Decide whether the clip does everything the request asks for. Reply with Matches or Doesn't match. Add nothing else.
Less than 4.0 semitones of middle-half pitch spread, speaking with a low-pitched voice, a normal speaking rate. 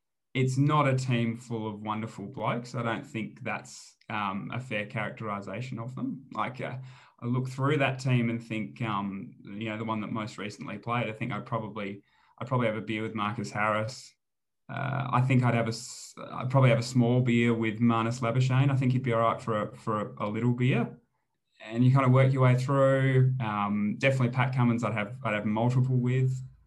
Doesn't match